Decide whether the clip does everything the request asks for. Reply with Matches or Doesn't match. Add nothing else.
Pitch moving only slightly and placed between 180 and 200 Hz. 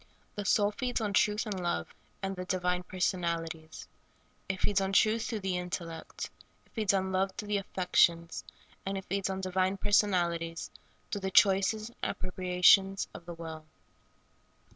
Matches